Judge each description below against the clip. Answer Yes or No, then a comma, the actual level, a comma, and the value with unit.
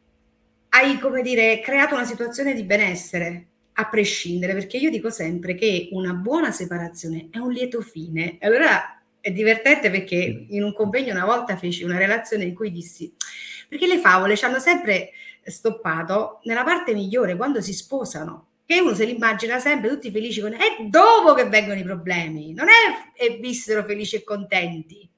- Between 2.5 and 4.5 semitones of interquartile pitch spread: No, wide, 5.5 semitones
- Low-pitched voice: No, high, 215 Hz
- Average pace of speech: No, fast, 175 wpm